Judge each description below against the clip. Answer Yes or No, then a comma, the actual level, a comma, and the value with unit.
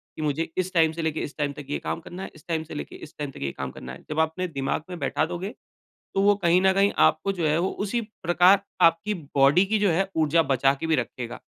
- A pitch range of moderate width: Yes, average, 3.9 semitones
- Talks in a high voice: No, medium, 160 Hz